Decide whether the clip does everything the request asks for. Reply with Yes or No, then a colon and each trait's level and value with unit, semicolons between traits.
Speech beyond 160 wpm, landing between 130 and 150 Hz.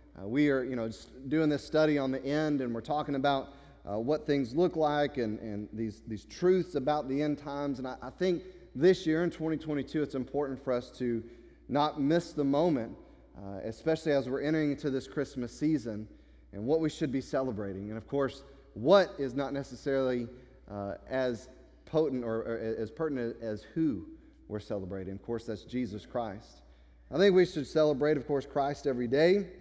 Yes: average, 195 wpm; medium, 140 Hz